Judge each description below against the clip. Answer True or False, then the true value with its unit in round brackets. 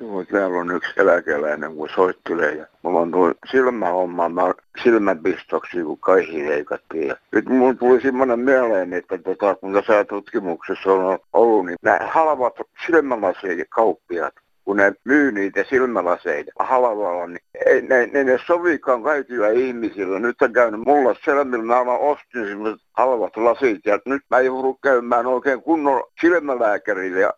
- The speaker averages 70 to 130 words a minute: False (145 wpm)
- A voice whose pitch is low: True (125 Hz)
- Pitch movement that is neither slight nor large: False (6.1 semitones)